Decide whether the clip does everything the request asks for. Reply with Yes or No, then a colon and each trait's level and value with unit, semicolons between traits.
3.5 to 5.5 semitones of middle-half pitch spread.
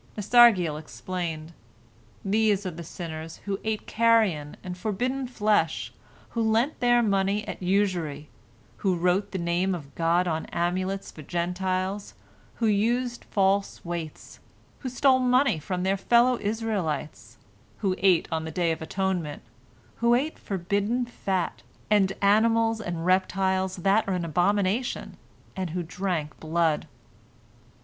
Yes: average, 4.1 semitones